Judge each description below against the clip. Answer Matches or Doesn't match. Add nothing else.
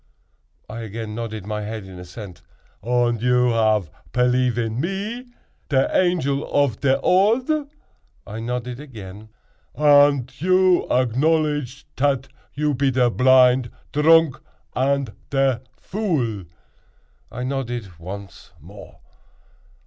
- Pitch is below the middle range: Matches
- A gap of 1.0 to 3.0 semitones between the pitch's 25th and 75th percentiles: Doesn't match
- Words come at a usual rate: Doesn't match